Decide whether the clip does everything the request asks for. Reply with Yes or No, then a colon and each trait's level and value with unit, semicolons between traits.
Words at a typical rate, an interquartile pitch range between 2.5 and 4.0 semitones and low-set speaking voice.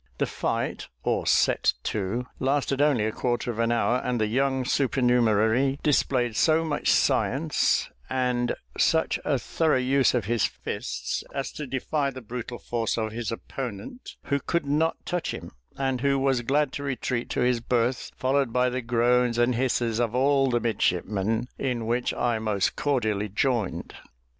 Yes: average, 165 wpm; average, 2.8 semitones; low, 125 Hz